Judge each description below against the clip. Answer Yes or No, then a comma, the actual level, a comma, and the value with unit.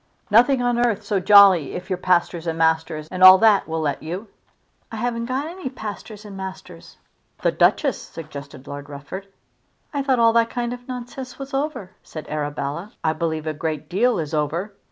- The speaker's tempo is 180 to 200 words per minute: Yes, average, 185 wpm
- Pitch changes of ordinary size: No, wide, 7.0 semitones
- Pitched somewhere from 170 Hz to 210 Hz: Yes, high, 190 Hz